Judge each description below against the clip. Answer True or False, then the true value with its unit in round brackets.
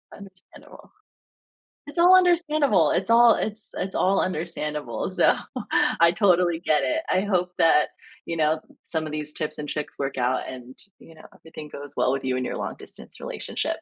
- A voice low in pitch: False (170 Hz)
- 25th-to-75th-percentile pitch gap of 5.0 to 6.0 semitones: True (5.5 semitones)